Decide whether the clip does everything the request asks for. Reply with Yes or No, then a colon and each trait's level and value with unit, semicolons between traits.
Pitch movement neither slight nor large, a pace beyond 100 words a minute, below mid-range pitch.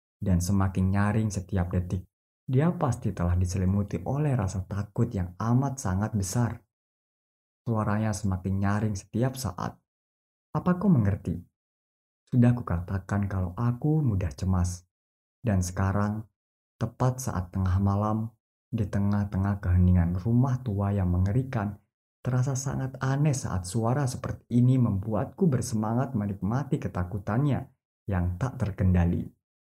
Yes: average, 4.6 semitones; average, 115 wpm; low, 105 Hz